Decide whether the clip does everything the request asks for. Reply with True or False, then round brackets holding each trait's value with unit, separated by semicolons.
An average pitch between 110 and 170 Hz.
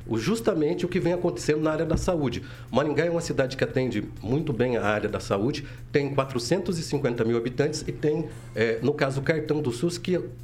True (140 Hz)